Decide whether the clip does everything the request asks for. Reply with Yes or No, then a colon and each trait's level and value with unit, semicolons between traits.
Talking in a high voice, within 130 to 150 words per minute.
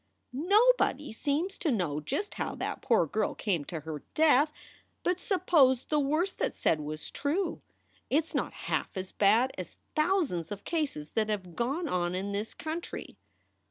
No: very high, 260 Hz; average, 170 wpm